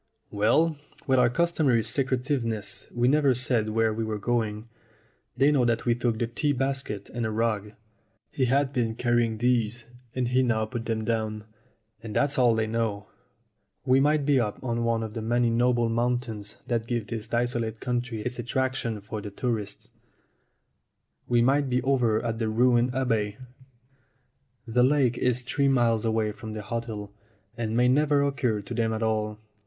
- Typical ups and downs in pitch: No, narrow, 2.3 semitones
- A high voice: No, low, 120 Hz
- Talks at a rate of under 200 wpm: Yes, average, 170 wpm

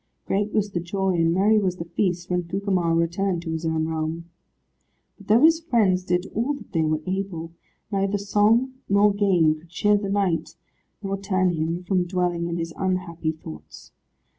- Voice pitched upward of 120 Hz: Yes, medium, 185 Hz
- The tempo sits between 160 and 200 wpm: Yes, average, 180 wpm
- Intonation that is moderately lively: Yes, average, 3.1 semitones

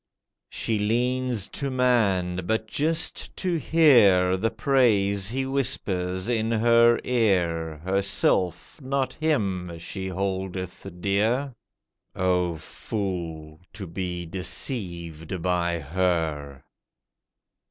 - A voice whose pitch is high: No, very low, 95 Hz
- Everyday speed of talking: No, slow, 90 wpm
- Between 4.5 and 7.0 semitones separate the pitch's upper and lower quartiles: Yes, average, 5.0 semitones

